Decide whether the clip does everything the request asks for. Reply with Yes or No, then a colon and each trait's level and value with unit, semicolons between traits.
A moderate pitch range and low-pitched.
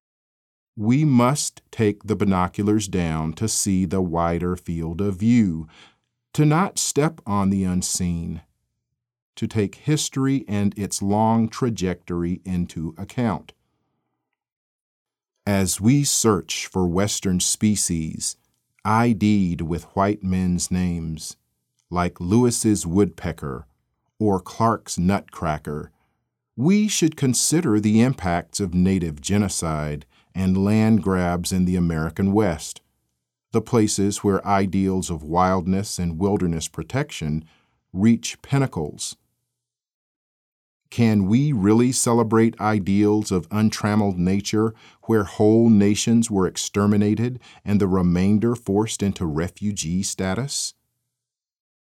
Yes: average, 4.2 semitones; low, 100 Hz